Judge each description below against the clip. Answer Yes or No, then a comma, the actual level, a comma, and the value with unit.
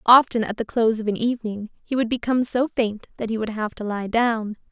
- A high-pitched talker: Yes, high, 225 Hz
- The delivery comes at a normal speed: No, fast, 240 wpm